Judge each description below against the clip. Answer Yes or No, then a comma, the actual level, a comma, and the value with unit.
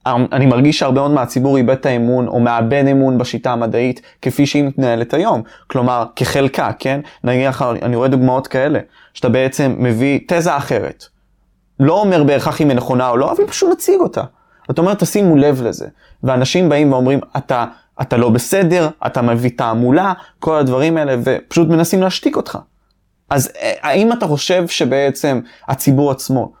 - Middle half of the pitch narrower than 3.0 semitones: No, average, 3.3 semitones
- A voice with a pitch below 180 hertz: Yes, low, 135 Hz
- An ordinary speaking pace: No, fast, 160 wpm